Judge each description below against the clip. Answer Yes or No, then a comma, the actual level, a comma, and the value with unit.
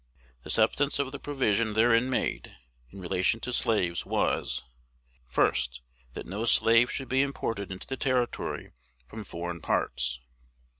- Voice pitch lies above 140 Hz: No, low, 110 Hz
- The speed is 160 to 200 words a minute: No, average, 140 wpm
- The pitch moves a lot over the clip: Yes, wide, 6.6 semitones